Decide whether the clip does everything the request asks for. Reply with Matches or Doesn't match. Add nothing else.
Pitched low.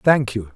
Matches